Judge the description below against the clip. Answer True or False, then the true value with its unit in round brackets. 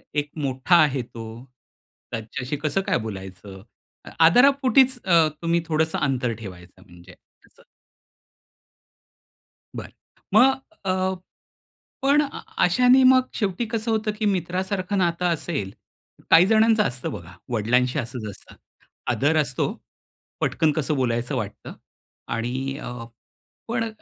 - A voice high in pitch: False (155 Hz)